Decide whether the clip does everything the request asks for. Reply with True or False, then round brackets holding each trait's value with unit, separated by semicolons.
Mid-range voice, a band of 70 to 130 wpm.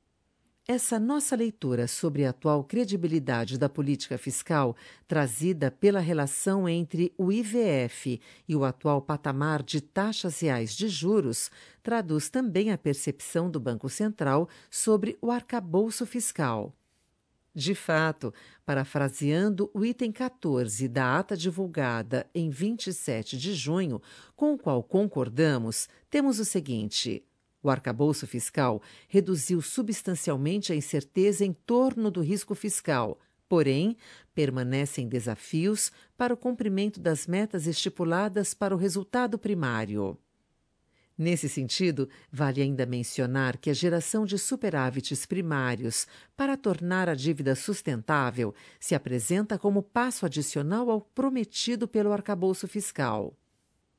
True (170 Hz; 120 wpm)